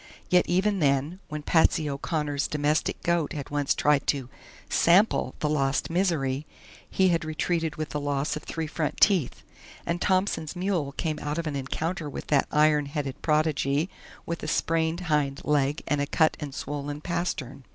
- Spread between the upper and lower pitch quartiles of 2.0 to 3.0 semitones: Yes, average, 2.7 semitones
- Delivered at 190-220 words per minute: No, average, 170 wpm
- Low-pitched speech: No, medium, 150 Hz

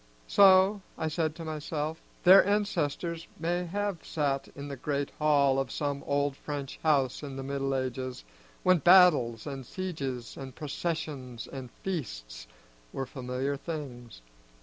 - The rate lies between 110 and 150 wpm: Yes, average, 140 wpm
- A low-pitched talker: No, medium, 145 Hz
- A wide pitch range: No, average, 3.8 semitones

